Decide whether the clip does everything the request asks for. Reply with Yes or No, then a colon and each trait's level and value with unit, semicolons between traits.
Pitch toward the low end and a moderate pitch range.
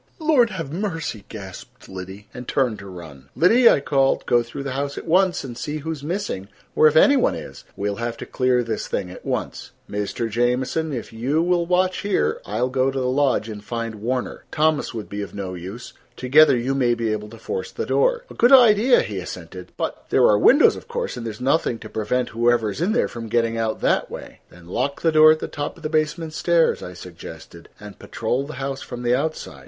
No: low, 125 Hz; wide, 6.6 semitones